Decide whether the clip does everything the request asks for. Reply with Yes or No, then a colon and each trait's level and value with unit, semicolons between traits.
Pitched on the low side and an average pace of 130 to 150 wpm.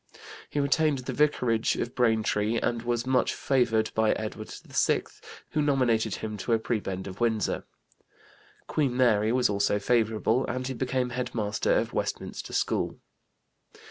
Yes: low, 120 Hz; average, 145 wpm